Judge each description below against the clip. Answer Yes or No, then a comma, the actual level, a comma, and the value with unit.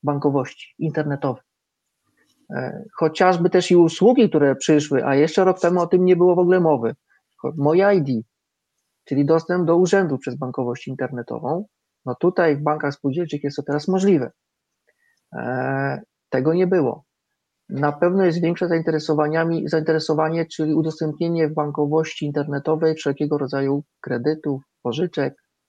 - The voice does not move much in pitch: No, average, 3.5 semitones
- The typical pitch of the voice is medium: Yes, medium, 155 Hz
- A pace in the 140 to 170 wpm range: No, average, 125 wpm